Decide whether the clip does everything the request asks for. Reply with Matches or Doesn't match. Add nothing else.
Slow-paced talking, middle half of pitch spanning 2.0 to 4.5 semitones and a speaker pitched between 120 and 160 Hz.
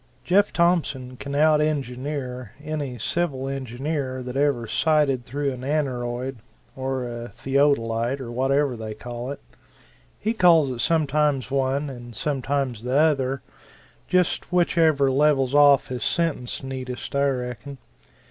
Matches